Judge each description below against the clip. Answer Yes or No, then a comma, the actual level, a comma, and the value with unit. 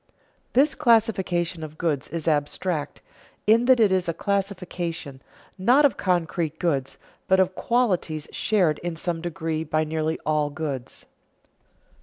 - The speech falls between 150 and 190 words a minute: No, slow, 135 wpm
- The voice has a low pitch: No, medium, 170 Hz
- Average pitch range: Yes, average, 3.9 semitones